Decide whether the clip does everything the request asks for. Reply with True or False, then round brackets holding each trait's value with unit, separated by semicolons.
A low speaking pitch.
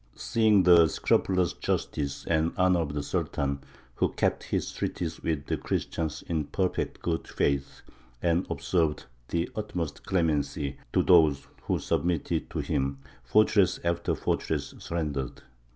True (80 Hz)